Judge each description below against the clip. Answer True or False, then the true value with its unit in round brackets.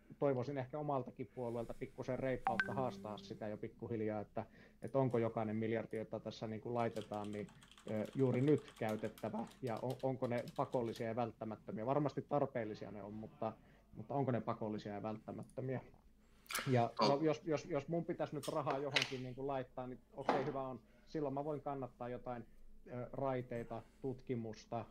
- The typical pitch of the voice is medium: False (125 Hz)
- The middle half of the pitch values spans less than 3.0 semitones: False (3.6 semitones)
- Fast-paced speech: True (160 wpm)